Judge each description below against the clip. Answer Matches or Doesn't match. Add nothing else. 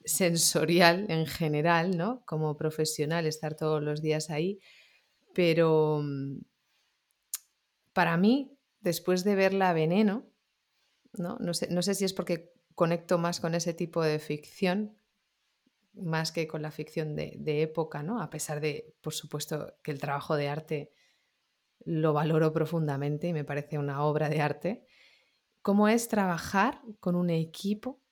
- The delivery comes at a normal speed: Matches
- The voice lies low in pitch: Doesn't match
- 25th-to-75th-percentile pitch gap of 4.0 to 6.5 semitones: Doesn't match